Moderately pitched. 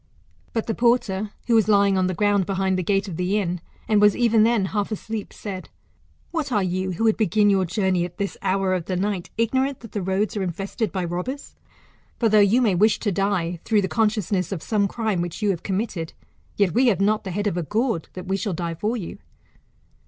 No: high, 200 Hz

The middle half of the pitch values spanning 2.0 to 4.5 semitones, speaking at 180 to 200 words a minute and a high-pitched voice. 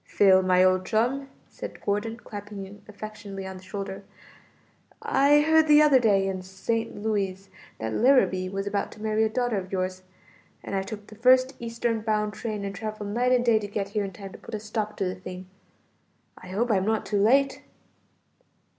Yes: average, 2.9 semitones; average, 195 wpm; high, 210 Hz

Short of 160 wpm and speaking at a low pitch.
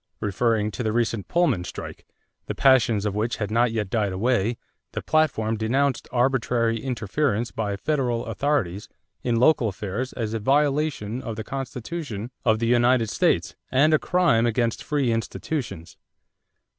Yes: average, 150 wpm; low, 115 Hz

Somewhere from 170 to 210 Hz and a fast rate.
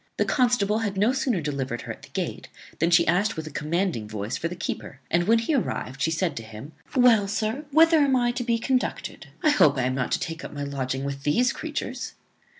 Yes: medium, 185 Hz; fast, 235 wpm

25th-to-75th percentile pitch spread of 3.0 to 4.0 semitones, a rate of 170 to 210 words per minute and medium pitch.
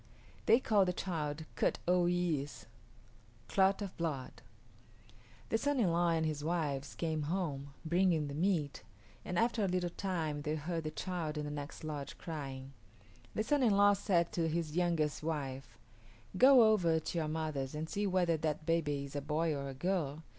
Yes: average, 3.5 semitones; average, 180 wpm; medium, 160 Hz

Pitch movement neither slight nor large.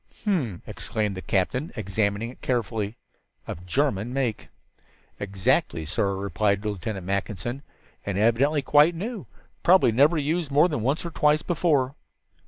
No: wide, 6.8 semitones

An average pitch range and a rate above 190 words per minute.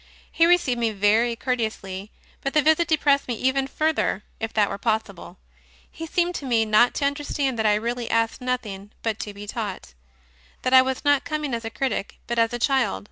Yes: average, 4.4 semitones; fast, 205 wpm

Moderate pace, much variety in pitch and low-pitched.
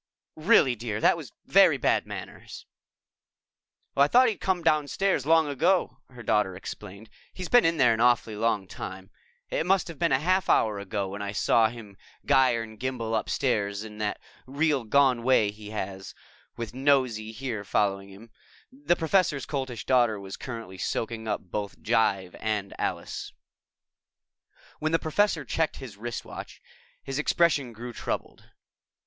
Yes: average, 155 wpm; wide, 5.7 semitones; low, 120 Hz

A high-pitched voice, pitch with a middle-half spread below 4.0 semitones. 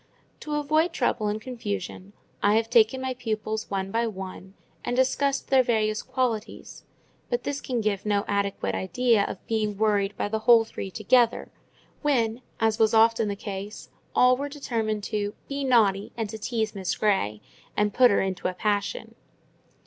Yes: high, 220 Hz; average, 3.4 semitones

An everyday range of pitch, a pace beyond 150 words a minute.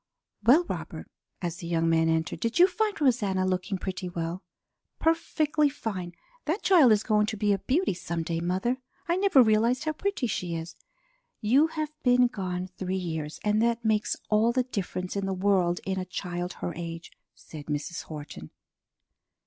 No: wide, 6.2 semitones; average, 175 wpm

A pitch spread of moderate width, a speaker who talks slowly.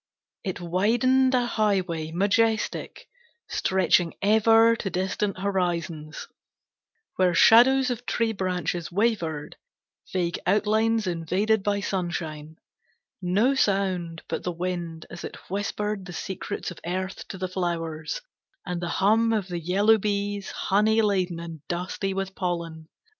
Yes: average, 3.5 semitones; slow, 125 wpm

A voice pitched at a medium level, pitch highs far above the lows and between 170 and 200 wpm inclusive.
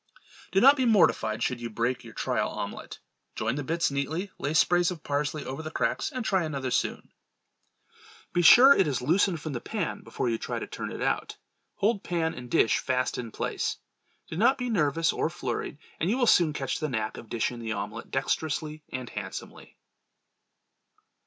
Yes: medium, 155 Hz; wide, 5.9 semitones; average, 190 wpm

